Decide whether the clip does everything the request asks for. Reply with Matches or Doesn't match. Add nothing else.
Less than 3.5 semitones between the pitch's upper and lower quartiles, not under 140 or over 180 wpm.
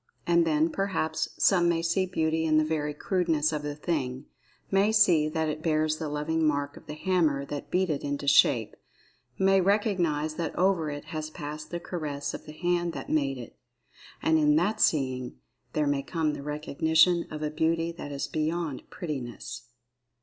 Matches